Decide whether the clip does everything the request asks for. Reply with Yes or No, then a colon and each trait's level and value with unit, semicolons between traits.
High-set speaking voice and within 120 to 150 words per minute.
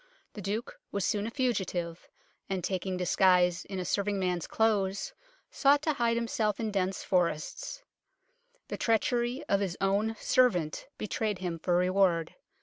Yes: high, 195 Hz; average, 145 wpm